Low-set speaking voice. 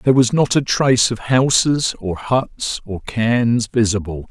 Yes: low, 115 Hz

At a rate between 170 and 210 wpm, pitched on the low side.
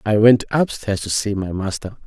Yes: fast, 205 wpm; low, 105 Hz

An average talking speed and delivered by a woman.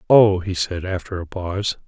No: average, 190 wpm; male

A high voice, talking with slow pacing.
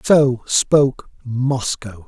No: low, 125 Hz; slow, 85 wpm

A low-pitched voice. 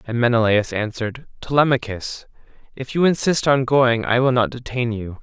Yes: low, 125 Hz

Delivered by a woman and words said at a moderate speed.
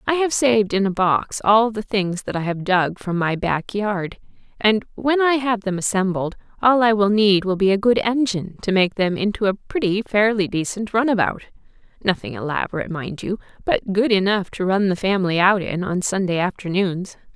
Yes: female; average, 195 wpm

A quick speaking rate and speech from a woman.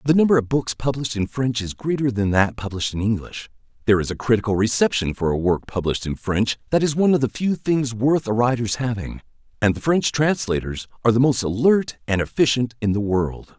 No: fast, 215 wpm; male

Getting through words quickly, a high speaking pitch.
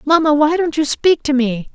Yes: fast, 240 wpm; very high, 295 Hz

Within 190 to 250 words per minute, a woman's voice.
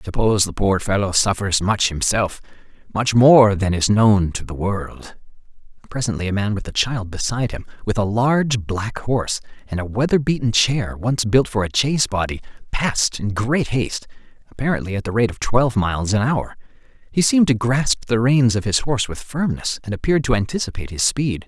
No: average, 195 wpm; male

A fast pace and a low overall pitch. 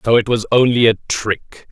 Yes: fast, 210 wpm; low, 115 Hz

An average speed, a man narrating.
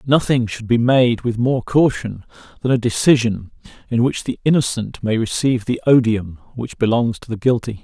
Yes: average, 175 wpm; male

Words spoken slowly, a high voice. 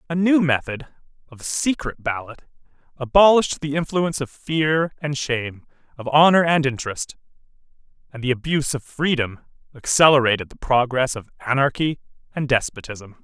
No: slow, 130 wpm; medium, 140 Hz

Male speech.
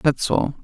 No: female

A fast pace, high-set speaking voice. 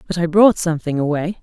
No: fast, 210 wpm; medium, 170 Hz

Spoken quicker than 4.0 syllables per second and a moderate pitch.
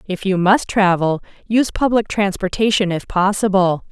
No: 4.9 syllables/s; high, 195 Hz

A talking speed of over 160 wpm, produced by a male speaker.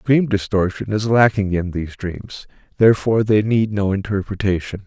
No: average, 150 wpm; male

